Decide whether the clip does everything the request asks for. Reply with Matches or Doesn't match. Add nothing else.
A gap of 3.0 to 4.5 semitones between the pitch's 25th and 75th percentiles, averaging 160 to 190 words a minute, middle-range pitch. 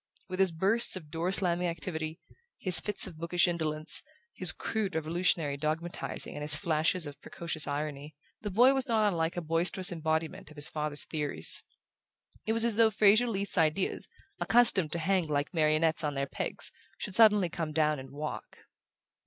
Matches